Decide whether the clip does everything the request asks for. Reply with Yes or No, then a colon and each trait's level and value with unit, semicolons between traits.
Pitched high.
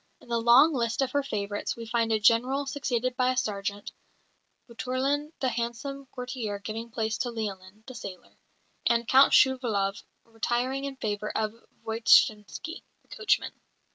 Yes: high, 235 Hz